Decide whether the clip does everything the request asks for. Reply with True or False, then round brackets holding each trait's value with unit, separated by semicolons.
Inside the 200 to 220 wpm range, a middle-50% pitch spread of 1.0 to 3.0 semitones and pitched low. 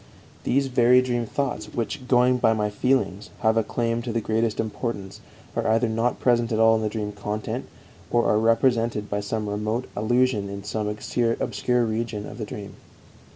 False (180 wpm; 2.4 semitones; 115 Hz)